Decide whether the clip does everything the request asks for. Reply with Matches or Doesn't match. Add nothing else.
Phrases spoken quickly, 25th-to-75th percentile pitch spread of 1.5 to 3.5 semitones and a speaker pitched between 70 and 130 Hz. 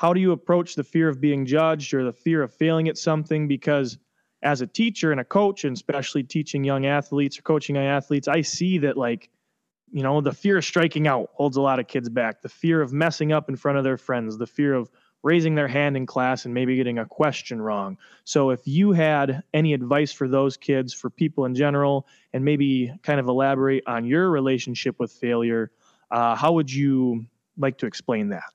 Doesn't match